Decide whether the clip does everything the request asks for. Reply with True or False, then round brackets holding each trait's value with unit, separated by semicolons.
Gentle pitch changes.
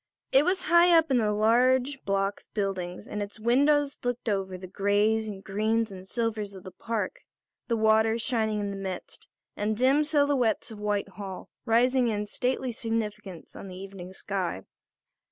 False (3.8 semitones)